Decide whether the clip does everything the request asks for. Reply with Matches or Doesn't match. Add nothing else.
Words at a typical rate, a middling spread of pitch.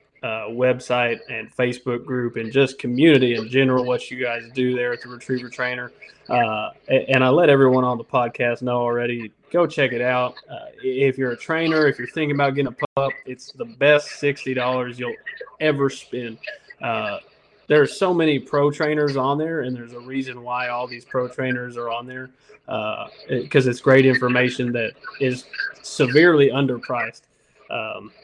Doesn't match